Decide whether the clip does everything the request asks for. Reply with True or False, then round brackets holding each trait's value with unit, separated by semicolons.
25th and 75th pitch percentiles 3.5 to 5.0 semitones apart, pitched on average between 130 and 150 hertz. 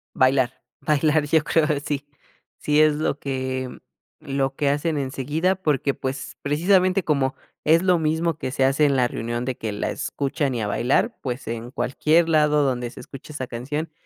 False (2.9 semitones; 140 Hz)